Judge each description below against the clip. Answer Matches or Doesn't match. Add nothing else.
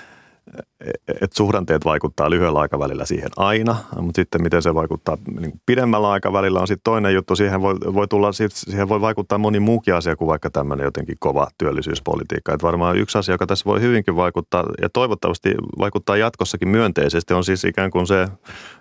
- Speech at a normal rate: Doesn't match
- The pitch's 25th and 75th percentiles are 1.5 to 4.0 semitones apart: Matches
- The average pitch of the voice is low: Matches